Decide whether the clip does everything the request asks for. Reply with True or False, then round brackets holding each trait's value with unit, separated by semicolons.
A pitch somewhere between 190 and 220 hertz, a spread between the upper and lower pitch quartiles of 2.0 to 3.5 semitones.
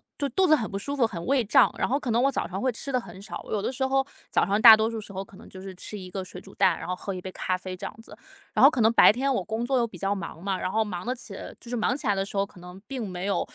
False (210 Hz; 4.9 semitones)